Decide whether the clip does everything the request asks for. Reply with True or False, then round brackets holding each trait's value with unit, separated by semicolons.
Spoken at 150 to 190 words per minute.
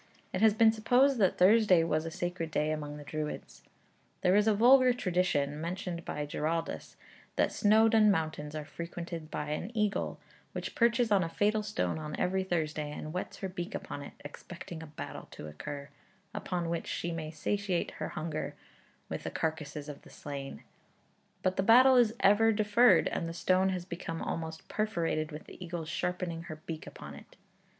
True (180 wpm)